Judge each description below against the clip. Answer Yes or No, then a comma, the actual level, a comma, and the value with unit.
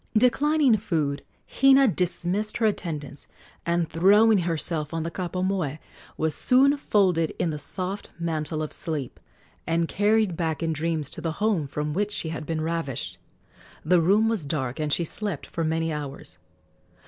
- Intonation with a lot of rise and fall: No, average, 4.7 semitones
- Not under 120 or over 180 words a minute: Yes, average, 160 wpm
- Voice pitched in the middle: Yes, medium, 170 Hz